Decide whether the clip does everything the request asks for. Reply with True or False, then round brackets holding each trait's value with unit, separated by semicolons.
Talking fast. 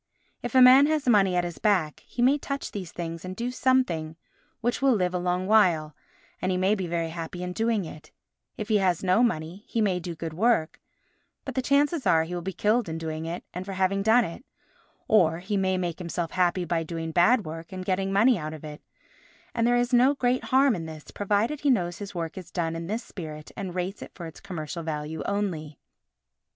True (225 wpm)